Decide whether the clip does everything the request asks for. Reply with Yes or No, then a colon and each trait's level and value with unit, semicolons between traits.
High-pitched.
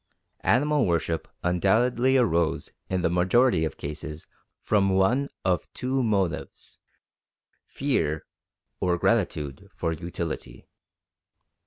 No: very low, 90 Hz